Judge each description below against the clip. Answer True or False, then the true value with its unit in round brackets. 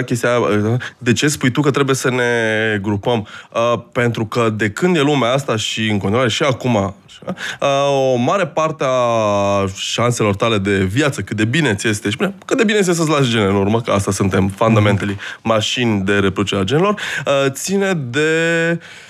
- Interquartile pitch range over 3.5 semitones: True (5.2 semitones)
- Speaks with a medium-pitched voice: False (120 Hz)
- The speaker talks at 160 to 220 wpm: True (170 wpm)